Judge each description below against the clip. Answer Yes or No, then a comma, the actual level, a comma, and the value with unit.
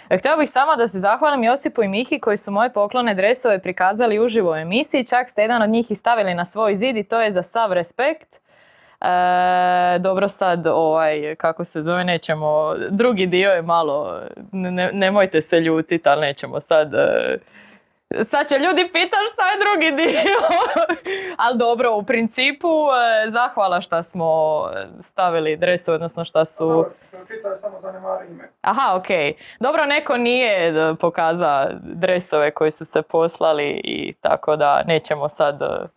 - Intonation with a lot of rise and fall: Yes, wide, 6.7 semitones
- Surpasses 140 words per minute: Yes, average, 150 wpm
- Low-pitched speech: No, high, 195 Hz